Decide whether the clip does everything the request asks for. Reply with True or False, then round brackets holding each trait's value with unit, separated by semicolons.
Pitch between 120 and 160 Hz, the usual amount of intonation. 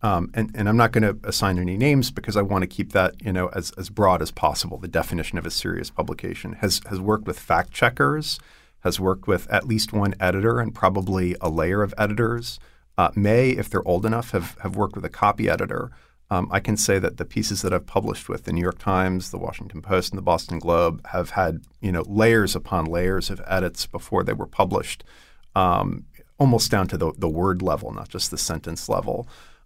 False (95 Hz; 3.1 semitones)